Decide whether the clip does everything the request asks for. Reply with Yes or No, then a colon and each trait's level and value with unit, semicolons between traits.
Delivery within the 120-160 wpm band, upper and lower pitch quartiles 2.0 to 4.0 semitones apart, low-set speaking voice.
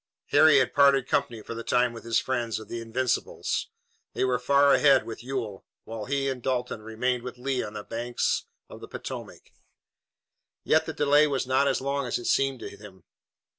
No: average, 195 wpm; average, 2.9 semitones; low, 125 Hz